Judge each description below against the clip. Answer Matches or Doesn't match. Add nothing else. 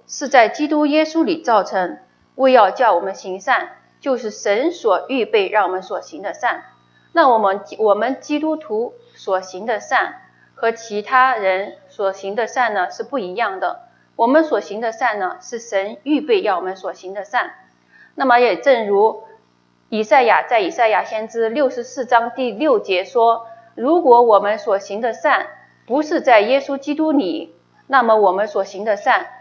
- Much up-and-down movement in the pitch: Matches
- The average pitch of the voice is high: Matches